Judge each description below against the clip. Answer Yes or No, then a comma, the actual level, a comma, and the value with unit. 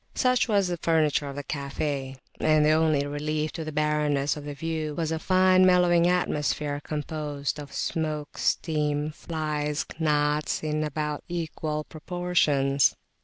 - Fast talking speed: No, average, 155 wpm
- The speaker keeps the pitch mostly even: Yes, narrow, 1.7 semitones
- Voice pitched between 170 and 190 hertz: No, medium, 150 Hz